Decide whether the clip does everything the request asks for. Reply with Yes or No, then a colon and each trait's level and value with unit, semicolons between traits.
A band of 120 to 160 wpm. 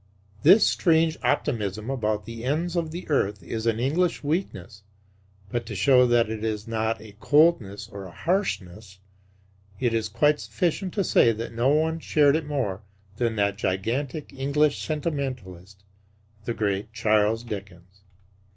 Yes: average, 150 wpm